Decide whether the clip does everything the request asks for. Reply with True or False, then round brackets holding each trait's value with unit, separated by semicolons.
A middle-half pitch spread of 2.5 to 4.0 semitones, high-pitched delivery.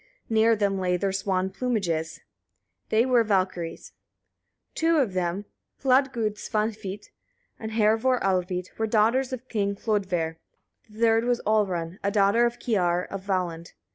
True (3.6 semitones; 205 Hz)